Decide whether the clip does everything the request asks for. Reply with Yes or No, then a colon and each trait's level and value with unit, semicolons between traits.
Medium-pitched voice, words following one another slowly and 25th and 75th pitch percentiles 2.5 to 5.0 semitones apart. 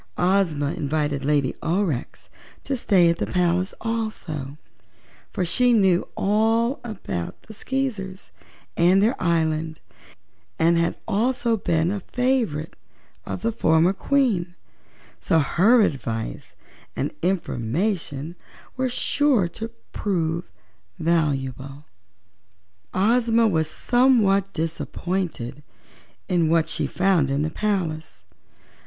No: medium, 180 Hz; slow, 105 wpm; wide, 5.5 semitones